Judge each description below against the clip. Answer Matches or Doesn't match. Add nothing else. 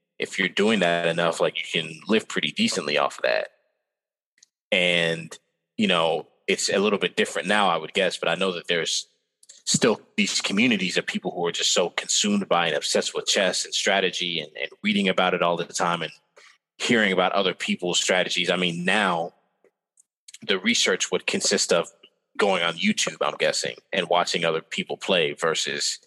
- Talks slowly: Doesn't match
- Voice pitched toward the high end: Matches